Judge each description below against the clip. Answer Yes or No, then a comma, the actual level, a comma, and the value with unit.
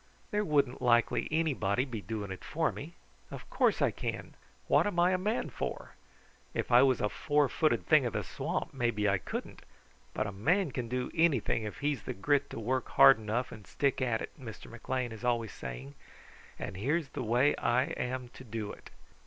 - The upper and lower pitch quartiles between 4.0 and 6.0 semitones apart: Yes, average, 4.6 semitones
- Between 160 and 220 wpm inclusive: Yes, average, 200 wpm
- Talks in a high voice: No, low, 125 Hz